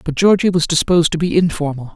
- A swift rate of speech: Yes, fast, 215 wpm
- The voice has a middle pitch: Yes, medium, 165 Hz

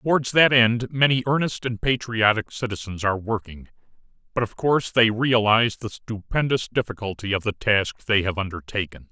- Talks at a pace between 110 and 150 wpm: No, average, 160 wpm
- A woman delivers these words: No, male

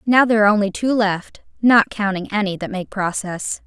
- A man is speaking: No, female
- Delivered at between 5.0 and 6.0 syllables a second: Yes, 5.4 syllables/s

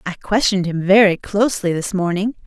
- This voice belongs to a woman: Yes, female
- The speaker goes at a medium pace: Yes, average, 170 wpm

